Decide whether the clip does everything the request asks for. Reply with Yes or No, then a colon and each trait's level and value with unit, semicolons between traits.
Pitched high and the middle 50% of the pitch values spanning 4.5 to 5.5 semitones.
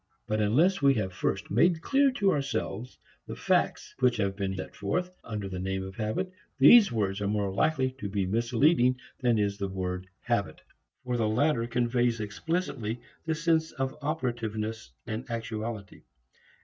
No: low, 115 Hz; average, 5.2 semitones